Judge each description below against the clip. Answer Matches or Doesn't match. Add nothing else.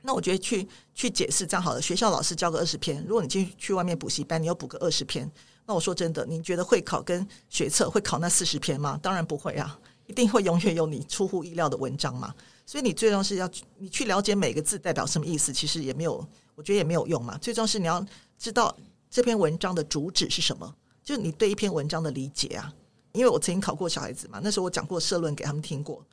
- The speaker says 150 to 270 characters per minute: Doesn't match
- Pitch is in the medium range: Matches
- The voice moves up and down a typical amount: Matches